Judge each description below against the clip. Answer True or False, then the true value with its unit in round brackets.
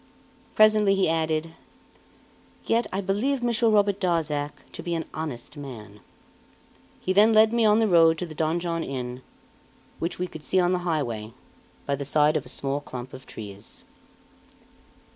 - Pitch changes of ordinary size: False (5.8 semitones)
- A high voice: False (165 Hz)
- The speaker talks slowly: False (160 wpm)